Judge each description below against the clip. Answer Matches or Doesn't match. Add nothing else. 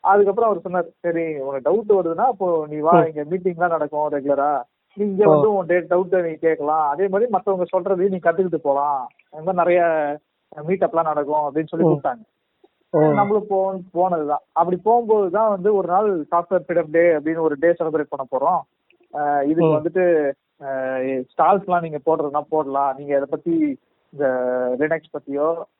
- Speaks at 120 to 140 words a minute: Matches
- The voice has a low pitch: Doesn't match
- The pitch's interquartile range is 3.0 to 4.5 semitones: Matches